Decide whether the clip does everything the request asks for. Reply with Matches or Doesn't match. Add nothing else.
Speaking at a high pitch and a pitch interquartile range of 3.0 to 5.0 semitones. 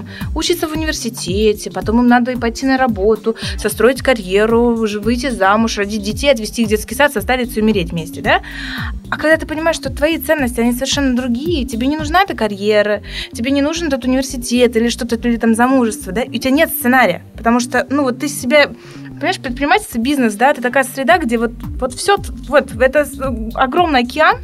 Matches